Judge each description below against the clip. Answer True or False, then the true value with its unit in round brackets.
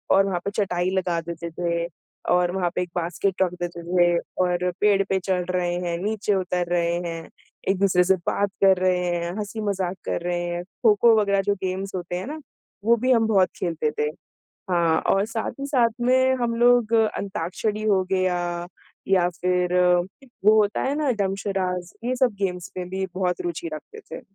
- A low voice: False (185 Hz)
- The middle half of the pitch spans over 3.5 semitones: False (2.8 semitones)